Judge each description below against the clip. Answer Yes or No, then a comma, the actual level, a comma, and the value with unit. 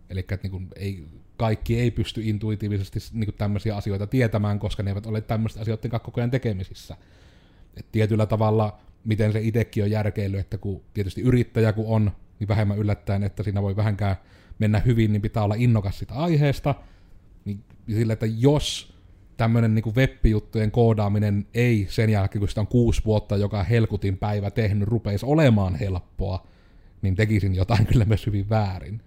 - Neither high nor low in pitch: No, low, 105 Hz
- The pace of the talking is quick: Yes, fast, 165 wpm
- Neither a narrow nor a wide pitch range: No, narrow, 2.0 semitones